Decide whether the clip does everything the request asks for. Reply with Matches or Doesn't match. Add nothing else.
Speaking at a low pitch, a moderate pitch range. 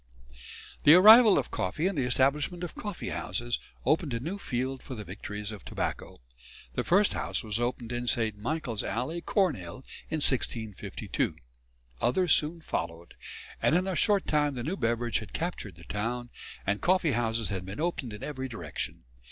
Doesn't match